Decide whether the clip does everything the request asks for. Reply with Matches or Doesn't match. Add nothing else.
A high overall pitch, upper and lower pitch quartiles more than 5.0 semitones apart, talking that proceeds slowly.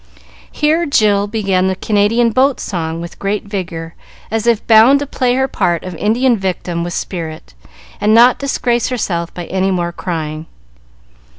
Doesn't match